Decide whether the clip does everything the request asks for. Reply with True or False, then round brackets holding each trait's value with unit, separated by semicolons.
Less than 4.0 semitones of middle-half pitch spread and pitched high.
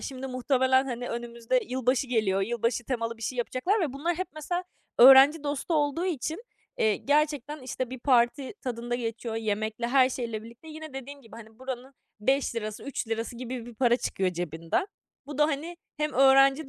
True (3.4 semitones; 255 Hz)